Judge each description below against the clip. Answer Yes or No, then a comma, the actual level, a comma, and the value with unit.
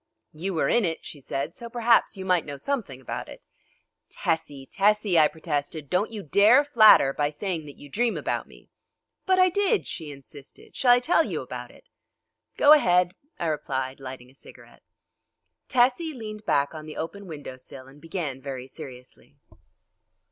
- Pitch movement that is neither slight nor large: No, wide, 7.9 semitones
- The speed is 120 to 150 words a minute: No, average, 175 wpm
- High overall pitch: No, medium, 165 Hz